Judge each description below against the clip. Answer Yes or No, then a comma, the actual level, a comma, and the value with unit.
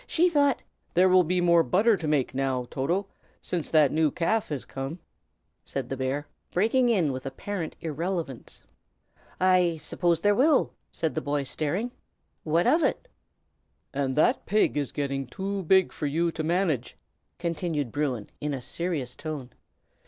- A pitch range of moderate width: Yes, average, 4.7 semitones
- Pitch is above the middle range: No, medium, 160 Hz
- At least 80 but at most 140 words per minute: No, average, 160 wpm